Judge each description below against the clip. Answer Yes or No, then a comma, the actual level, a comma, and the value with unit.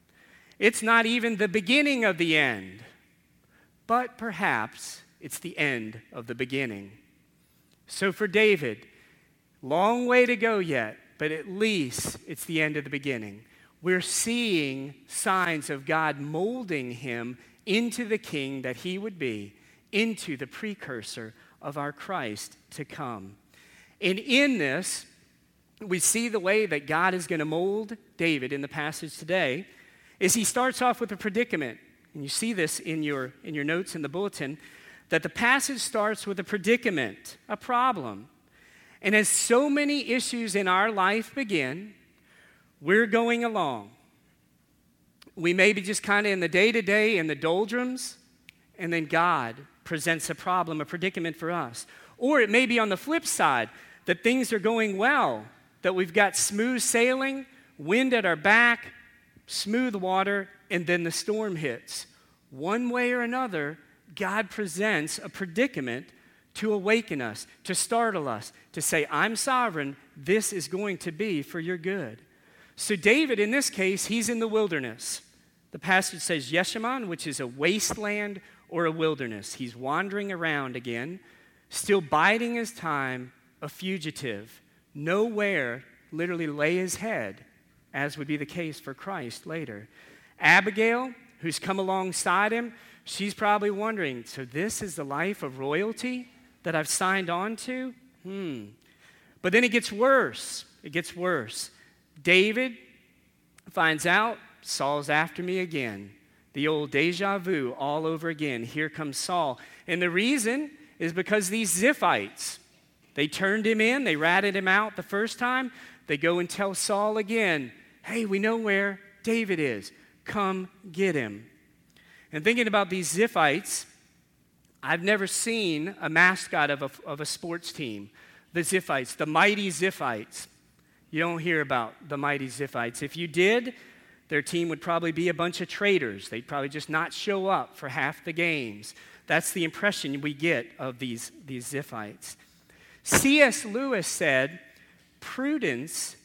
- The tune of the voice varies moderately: No, wide, 6.5 semitones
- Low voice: No, medium, 185 Hz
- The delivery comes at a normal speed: Yes, average, 155 wpm